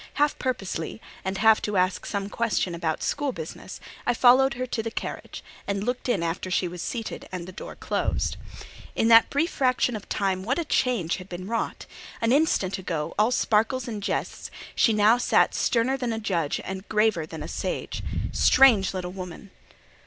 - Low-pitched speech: No, high, 210 Hz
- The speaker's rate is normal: Yes, average, 185 wpm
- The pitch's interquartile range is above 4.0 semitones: Yes, average, 4.9 semitones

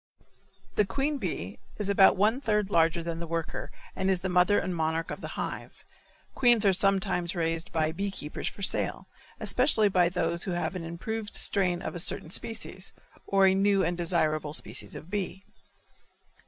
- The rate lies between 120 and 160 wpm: No, average, 180 wpm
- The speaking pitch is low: No, medium, 185 Hz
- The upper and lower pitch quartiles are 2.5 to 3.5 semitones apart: Yes, average, 3.1 semitones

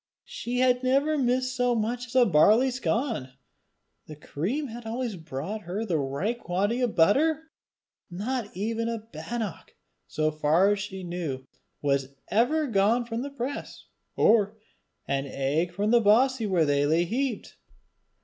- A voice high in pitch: Yes, high, 220 Hz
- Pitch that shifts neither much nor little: No, wide, 6.3 semitones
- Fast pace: No, average, 150 wpm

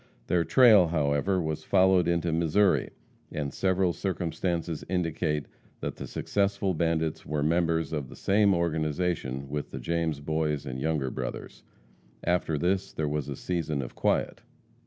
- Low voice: Yes, very low, 80 Hz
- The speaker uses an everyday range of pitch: Yes, average, 3.1 semitones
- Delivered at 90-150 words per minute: Yes, average, 145 wpm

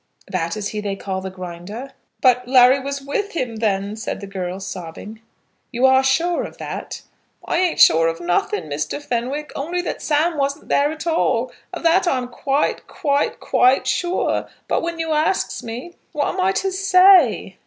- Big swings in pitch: Yes, wide, 8.3 semitones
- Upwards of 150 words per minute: Yes, average, 185 wpm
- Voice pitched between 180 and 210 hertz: No, very high, 265 Hz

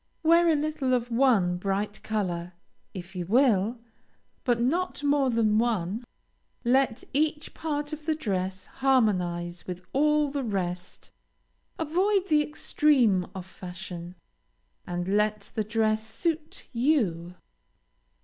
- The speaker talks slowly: Yes, slow, 120 wpm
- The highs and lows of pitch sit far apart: Yes, wide, 7.8 semitones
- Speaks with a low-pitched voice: No, high, 225 Hz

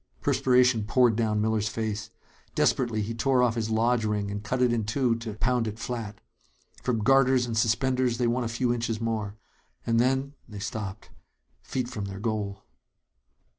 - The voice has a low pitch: Yes, low, 115 Hz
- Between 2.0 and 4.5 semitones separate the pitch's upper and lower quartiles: Yes, narrow, 2.6 semitones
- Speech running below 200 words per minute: Yes, average, 170 wpm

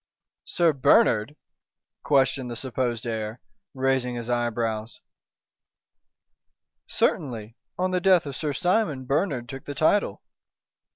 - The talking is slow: Yes, slow, 110 wpm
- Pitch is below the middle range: Yes, low, 130 Hz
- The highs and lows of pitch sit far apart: No, average, 4.1 semitones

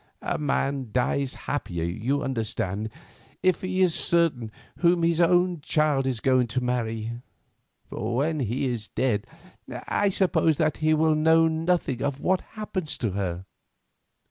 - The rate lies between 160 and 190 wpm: No, average, 145 wpm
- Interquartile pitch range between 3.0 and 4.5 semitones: No, wide, 5.6 semitones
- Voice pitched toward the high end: No, medium, 140 Hz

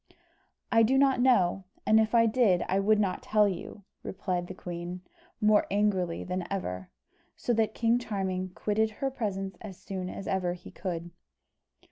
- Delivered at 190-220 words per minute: No, average, 165 wpm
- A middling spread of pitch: Yes, average, 3.3 semitones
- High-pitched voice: Yes, high, 195 Hz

